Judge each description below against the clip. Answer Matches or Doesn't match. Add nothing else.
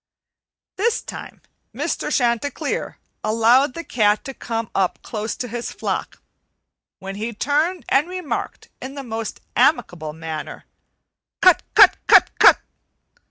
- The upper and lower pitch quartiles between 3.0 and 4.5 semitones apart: Doesn't match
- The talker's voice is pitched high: Matches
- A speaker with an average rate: Doesn't match